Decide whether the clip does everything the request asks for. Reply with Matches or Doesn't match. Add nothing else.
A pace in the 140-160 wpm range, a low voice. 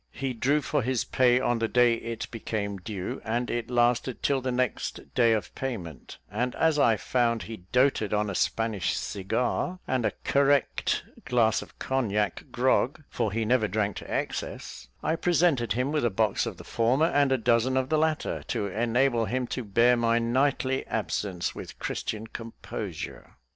Doesn't match